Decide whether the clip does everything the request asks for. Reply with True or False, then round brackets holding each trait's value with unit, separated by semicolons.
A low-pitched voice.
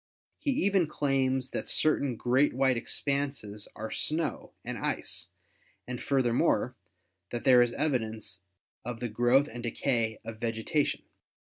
True (125 Hz)